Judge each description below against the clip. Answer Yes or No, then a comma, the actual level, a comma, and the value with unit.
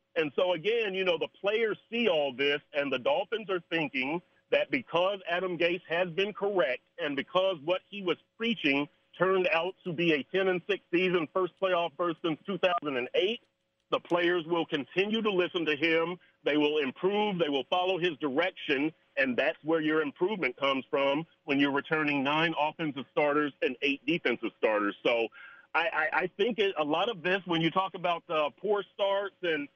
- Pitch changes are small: No, average, 4.0 semitones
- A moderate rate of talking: Yes, average, 190 wpm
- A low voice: No, medium, 175 Hz